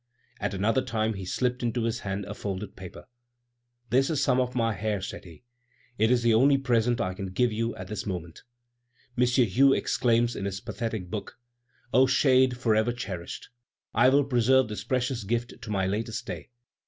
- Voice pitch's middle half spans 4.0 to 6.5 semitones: No, average, 3.6 semitones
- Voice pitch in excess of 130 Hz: No, low, 115 Hz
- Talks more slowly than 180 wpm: No, average, 185 wpm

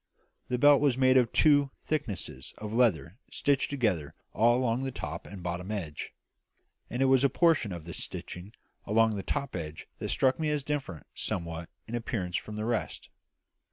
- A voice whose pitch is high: No, low, 115 Hz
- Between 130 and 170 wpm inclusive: No, average, 180 wpm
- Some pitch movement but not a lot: No, wide, 6.8 semitones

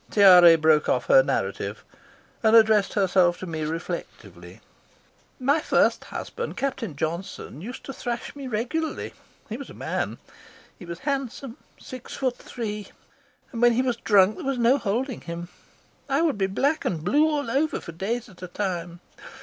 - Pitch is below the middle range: No, high, 220 Hz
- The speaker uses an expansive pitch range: Yes, wide, 6.8 semitones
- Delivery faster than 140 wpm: Yes, average, 165 wpm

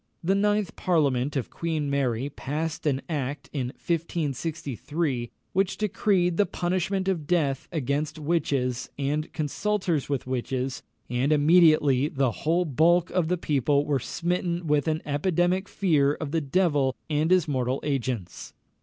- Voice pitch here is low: No, medium, 150 Hz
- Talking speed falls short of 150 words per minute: Yes, average, 140 wpm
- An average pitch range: Yes, average, 4.1 semitones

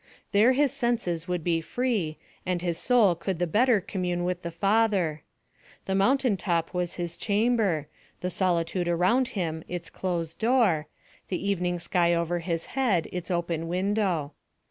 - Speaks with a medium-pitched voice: Yes, medium, 180 Hz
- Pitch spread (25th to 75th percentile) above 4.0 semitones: No, average, 3.6 semitones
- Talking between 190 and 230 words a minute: No, average, 155 wpm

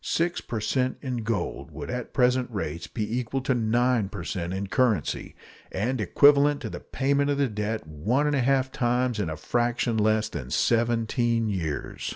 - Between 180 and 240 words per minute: Yes, average, 185 wpm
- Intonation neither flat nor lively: Yes, average, 3.4 semitones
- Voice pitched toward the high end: No, low, 120 Hz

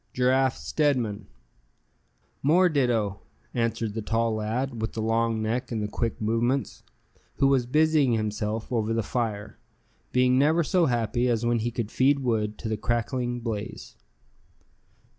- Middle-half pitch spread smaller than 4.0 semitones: Yes, average, 2.8 semitones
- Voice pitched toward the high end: No, low, 115 Hz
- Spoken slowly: No, average, 145 wpm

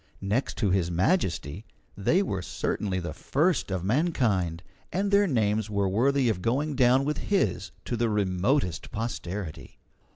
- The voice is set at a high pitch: No, low, 105 Hz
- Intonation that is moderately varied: No, wide, 6.9 semitones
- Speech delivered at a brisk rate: No, average, 150 wpm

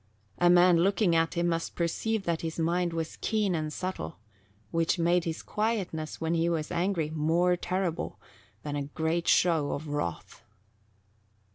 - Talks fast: No, average, 155 wpm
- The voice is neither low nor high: Yes, medium, 170 Hz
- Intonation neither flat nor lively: No, narrow, 1.9 semitones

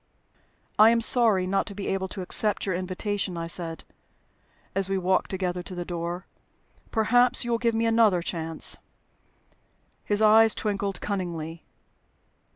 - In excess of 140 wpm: Yes, average, 150 wpm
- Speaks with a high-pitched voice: Yes, high, 195 Hz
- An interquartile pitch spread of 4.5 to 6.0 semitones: No, average, 3.5 semitones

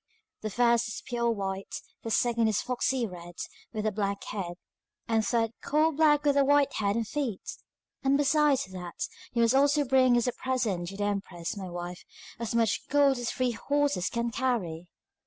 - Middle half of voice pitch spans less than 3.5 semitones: No, average, 5.0 semitones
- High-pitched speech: Yes, high, 235 Hz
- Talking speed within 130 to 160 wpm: No, average, 190 wpm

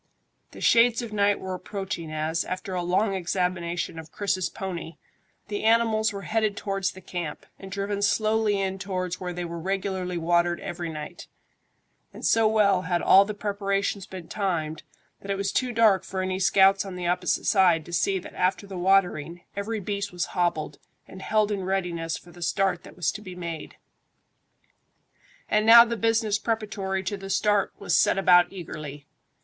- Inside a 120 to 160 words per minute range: No, average, 180 wpm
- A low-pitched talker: No, high, 190 Hz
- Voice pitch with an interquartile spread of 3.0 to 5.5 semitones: No, narrow, 2.5 semitones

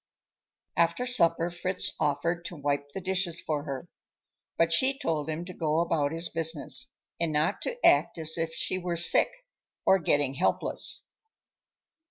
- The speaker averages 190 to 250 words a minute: No, average, 155 wpm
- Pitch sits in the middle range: Yes, medium, 165 Hz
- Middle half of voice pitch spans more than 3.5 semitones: No, narrow, 2.5 semitones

